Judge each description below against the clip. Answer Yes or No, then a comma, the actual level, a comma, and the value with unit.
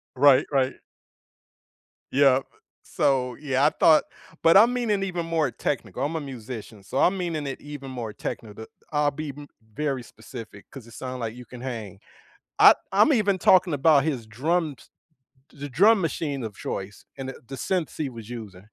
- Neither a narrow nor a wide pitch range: Yes, average, 4.8 semitones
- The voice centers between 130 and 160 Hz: Yes, low, 135 Hz